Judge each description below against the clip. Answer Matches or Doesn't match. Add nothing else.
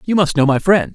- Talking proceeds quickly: Matches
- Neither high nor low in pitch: Matches